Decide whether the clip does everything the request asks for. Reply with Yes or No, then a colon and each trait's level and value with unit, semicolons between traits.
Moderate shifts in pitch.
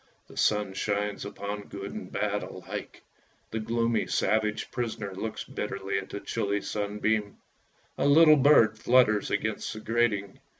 No: narrow, 2.1 semitones